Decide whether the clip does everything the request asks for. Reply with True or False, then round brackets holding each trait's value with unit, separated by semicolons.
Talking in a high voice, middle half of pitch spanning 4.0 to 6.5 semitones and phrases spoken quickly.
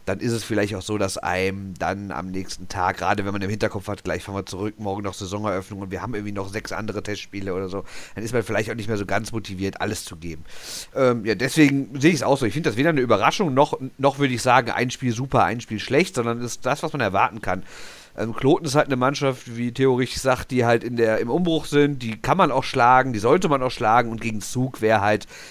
False (115 Hz; 4.4 semitones; 265 wpm)